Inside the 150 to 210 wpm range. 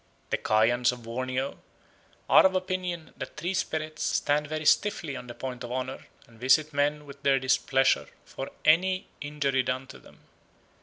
Yes: average, 165 wpm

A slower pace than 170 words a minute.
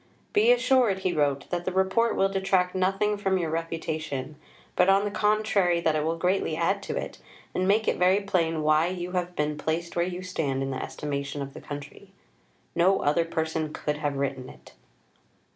No: average, 195 wpm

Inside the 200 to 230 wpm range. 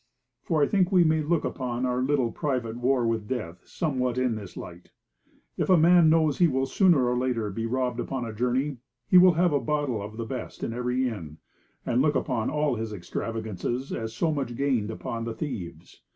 Yes: fast, 205 wpm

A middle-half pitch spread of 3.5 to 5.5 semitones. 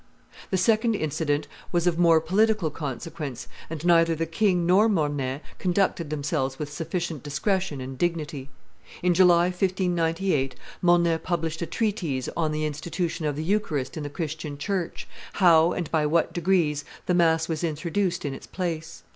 No: average, 2.9 semitones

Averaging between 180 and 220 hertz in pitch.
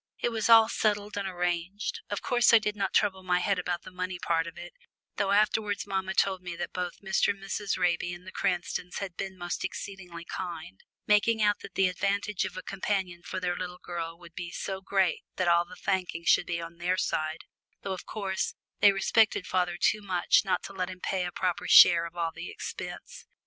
Yes: medium, 185 Hz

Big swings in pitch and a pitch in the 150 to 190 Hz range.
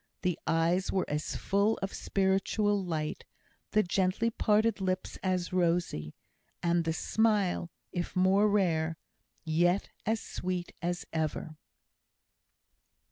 No: average, 2.9 semitones; medium, 185 Hz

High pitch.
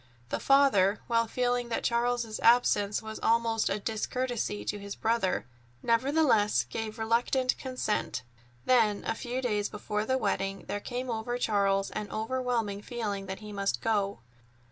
Yes: high, 225 Hz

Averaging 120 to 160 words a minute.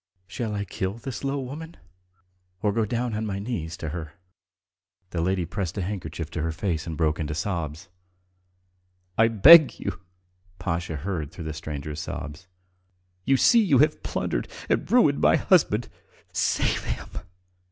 Yes: average, 155 wpm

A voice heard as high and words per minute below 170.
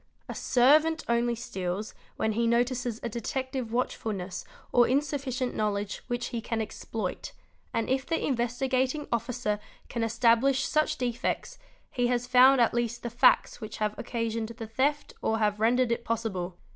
Yes: high, 235 Hz; average, 155 wpm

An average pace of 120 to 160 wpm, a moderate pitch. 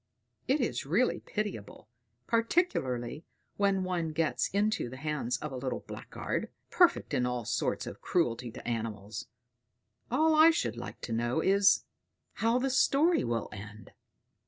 Yes: average, 145 wpm; medium, 160 Hz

